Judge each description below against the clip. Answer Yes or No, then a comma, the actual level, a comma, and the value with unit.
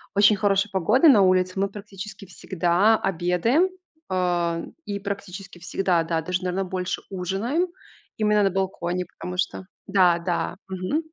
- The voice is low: No, high, 190 Hz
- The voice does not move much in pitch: Yes, narrow, 2.0 semitones